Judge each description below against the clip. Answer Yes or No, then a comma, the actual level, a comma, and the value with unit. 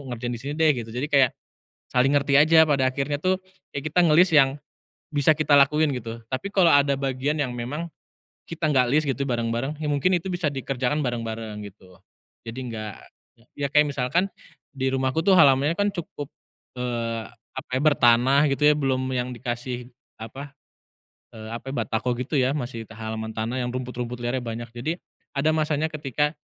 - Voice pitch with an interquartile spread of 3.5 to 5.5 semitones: Yes, average, 3.8 semitones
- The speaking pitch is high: No, low, 135 Hz